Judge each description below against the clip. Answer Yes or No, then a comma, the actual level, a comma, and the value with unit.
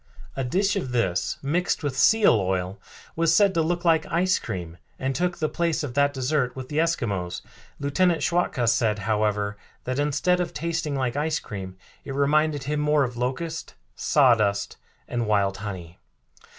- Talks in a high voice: No, medium, 140 Hz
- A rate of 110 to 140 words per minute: No, average, 165 wpm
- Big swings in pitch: Yes, wide, 7.2 semitones